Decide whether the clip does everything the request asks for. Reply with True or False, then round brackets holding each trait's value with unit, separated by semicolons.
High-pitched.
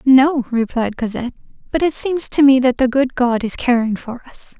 True (250 Hz)